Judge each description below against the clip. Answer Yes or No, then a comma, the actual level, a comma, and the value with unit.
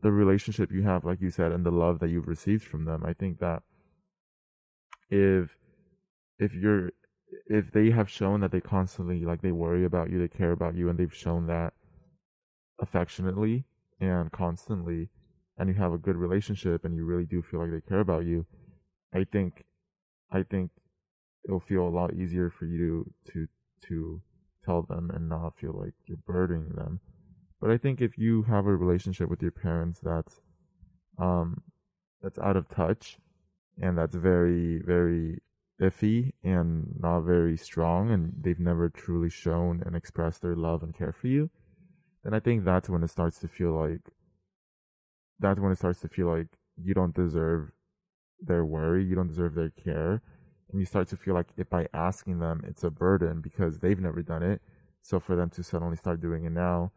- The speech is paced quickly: No, average, 185 wpm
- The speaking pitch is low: Yes, very low, 90 Hz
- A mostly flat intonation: Yes, narrow, 2.3 semitones